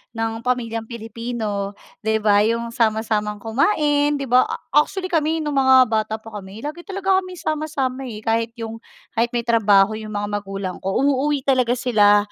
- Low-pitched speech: No, high, 230 Hz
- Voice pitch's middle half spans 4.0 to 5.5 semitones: Yes, average, 4.4 semitones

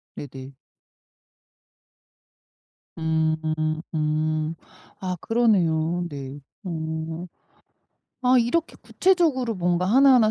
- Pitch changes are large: Yes, wide, 6.3 semitones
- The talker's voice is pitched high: No, medium, 165 Hz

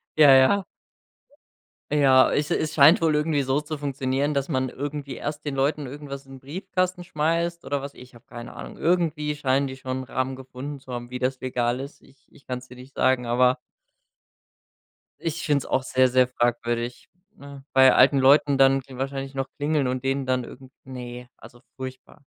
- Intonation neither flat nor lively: No, narrow, 2.2 semitones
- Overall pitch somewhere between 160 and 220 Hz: No, low, 135 Hz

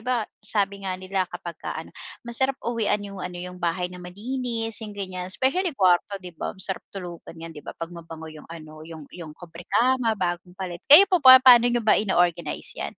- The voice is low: No, medium, 185 Hz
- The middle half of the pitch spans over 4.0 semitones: Yes, average, 4.7 semitones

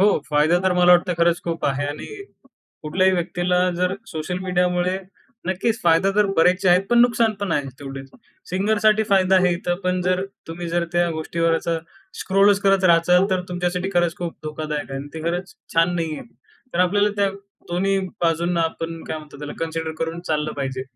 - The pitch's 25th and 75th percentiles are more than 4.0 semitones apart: No, narrow, 2.4 semitones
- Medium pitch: Yes, medium, 175 Hz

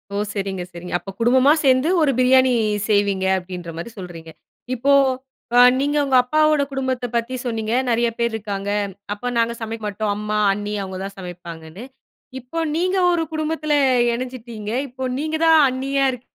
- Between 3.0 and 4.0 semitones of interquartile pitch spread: No, average, 4.7 semitones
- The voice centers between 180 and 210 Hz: No, high, 235 Hz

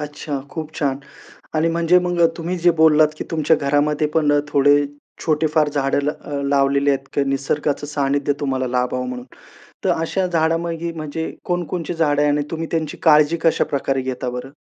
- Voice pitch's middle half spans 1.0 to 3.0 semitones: Yes, average, 2.7 semitones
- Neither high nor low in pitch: Yes, medium, 150 Hz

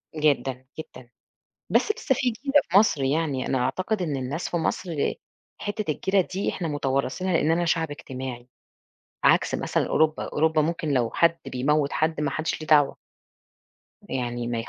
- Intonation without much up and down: No, average, 4.1 semitones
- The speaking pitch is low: No, medium, 155 Hz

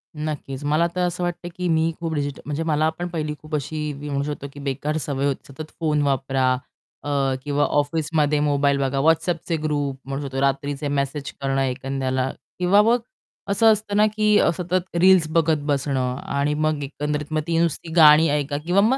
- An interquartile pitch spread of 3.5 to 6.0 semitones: No, average, 2.8 semitones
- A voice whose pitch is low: No, medium, 150 Hz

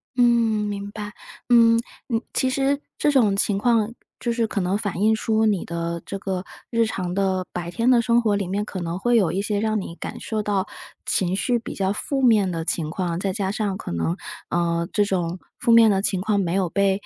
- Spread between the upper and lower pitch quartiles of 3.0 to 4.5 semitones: Yes, average, 3.5 semitones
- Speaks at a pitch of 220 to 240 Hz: No, high, 205 Hz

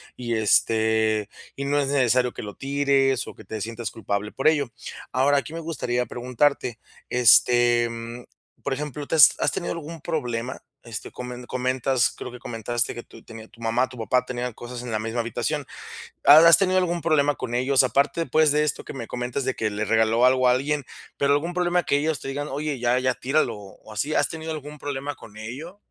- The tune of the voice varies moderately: Yes, average, 3.7 semitones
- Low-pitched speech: Yes, low, 125 Hz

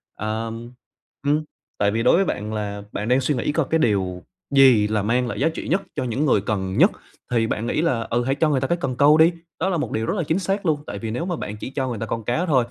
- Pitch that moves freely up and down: Yes, wide, 5.9 semitones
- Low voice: Yes, low, 125 Hz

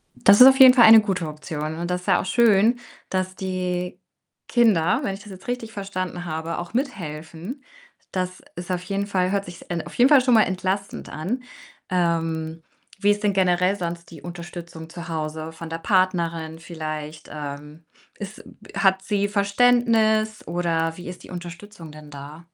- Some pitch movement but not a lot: Yes, average, 3.7 semitones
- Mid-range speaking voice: Yes, medium, 180 Hz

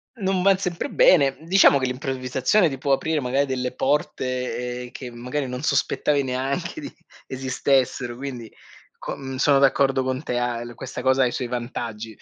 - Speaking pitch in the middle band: No, low, 130 Hz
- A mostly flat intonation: Yes, narrow, 2.2 semitones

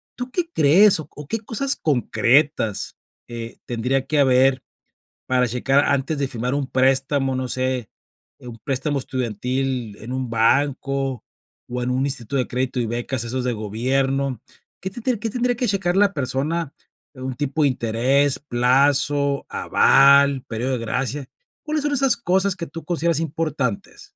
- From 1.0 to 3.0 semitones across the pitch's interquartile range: No, average, 3.6 semitones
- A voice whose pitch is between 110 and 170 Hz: Yes, low, 135 Hz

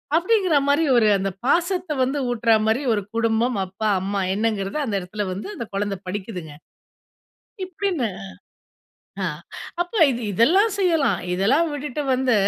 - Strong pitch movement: Yes, wide, 6.8 semitones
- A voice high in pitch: Yes, high, 235 Hz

